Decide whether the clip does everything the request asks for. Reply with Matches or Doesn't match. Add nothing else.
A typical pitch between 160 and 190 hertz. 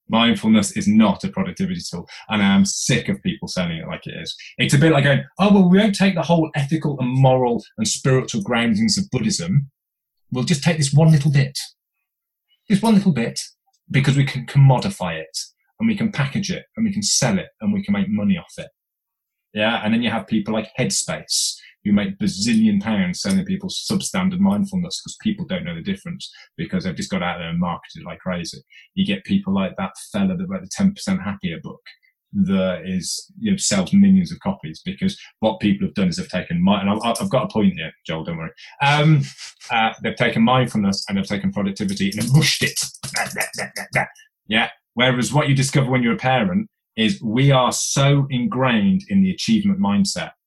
Matches